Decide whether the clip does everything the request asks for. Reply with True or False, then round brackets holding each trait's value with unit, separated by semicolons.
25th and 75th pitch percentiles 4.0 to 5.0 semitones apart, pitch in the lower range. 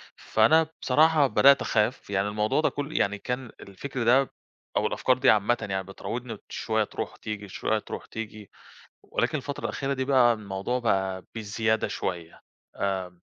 True (4.3 semitones; 110 Hz)